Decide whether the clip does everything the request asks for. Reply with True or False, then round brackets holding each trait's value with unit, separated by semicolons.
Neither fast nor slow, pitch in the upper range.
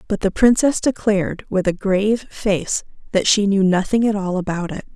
True (195 wpm; 200 Hz)